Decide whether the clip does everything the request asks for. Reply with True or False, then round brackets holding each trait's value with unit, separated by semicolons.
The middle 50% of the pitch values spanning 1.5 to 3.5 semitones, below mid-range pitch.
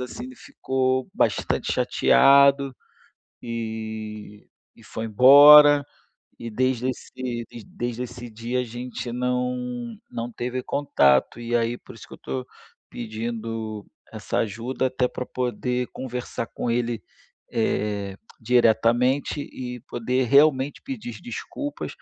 True (2.4 semitones; 125 Hz)